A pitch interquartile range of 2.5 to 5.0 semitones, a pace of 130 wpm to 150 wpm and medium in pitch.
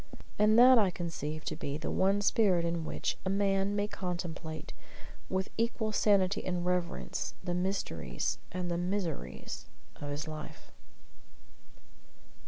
Yes: average, 4.0 semitones; slow, 135 wpm; medium, 180 Hz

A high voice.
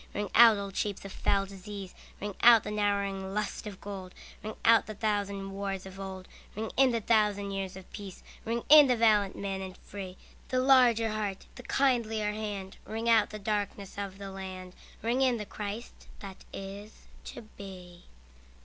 Yes: high, 205 Hz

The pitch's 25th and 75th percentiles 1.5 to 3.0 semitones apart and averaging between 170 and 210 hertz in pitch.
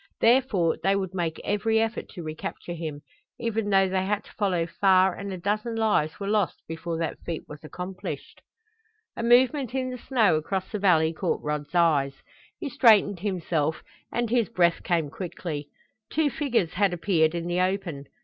No: average, 4.7 semitones; high, 190 Hz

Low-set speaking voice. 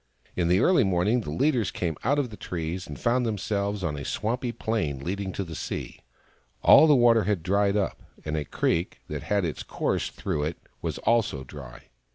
Yes: low, 100 Hz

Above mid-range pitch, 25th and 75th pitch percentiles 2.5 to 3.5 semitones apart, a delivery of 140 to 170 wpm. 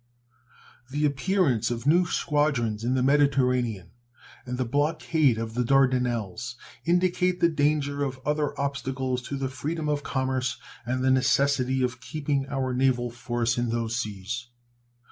No: low, 130 Hz; average, 3.0 semitones; average, 145 wpm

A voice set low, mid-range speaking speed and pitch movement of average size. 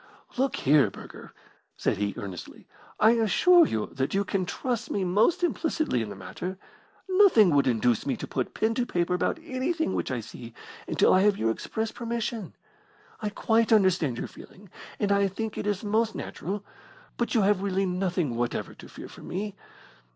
No: high, 200 Hz; average, 180 wpm; average, 4.7 semitones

